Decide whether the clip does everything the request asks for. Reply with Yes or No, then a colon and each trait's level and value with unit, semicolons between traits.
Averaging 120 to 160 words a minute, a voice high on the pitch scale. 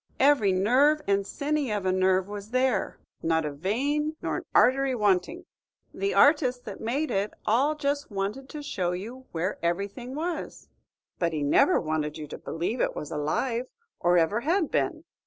No: average, 175 wpm; high, 220 Hz